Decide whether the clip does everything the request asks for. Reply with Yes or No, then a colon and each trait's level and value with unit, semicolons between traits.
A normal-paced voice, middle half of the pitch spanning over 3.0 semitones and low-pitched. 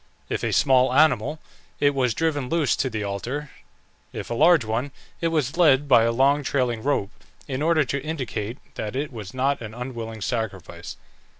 Yes: average, 180 wpm; average, 4.1 semitones; low, 130 Hz